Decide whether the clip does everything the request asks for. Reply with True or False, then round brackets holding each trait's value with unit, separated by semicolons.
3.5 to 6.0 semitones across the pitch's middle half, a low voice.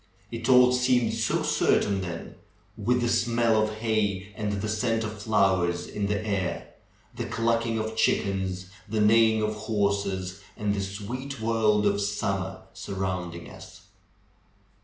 False (2.6 semitones; 105 Hz)